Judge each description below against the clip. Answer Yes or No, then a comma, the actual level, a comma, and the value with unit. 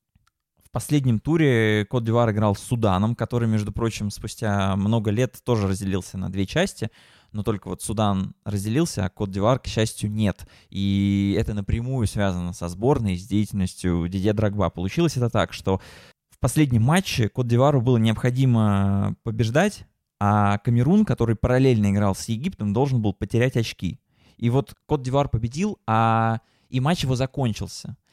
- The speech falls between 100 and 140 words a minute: No, average, 155 wpm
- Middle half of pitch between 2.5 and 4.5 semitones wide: Yes, average, 3.8 semitones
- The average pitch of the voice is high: No, low, 110 Hz